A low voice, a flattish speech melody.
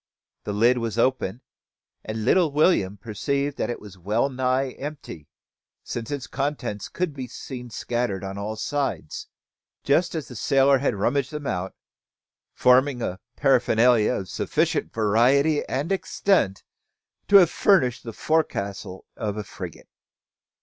No: low, 125 Hz; average, 4.9 semitones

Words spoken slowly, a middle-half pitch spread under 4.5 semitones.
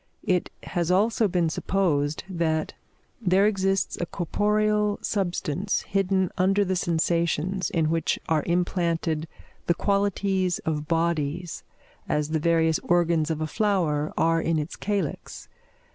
Yes: slow, 130 wpm; average, 3.2 semitones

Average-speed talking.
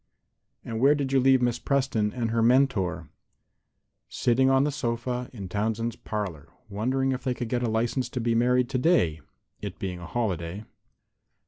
Yes: average, 165 wpm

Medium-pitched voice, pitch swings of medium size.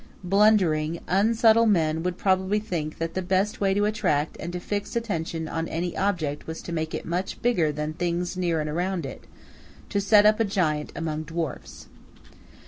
Yes: medium, 175 Hz; average, 4.0 semitones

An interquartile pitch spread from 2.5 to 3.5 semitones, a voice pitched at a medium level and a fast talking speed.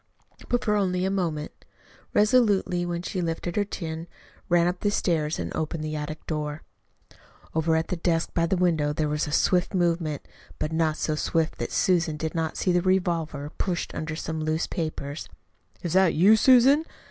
No: average, 2.8 semitones; medium, 165 Hz; average, 180 wpm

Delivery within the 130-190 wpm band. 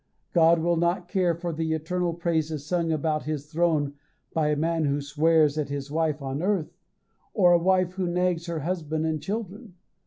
Yes: average, 185 wpm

